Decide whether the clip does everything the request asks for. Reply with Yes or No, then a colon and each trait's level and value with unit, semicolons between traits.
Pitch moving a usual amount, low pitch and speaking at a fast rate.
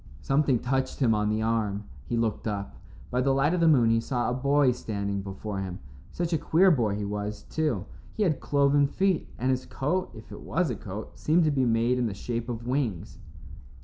Yes: average, 4.9 semitones; low, 125 Hz; fast, 215 wpm